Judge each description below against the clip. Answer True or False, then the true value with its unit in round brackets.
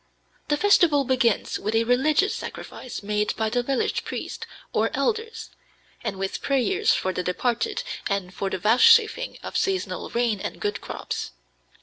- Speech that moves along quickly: False (150 wpm)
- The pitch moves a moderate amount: False (8.8 semitones)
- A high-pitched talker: True (245 Hz)